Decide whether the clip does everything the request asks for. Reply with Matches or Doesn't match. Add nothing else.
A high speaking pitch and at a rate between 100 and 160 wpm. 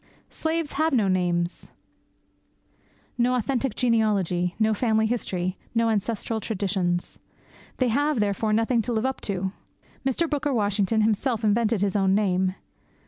Matches